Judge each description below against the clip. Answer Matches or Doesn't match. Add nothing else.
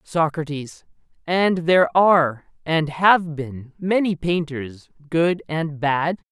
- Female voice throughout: Doesn't match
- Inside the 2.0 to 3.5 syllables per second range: Matches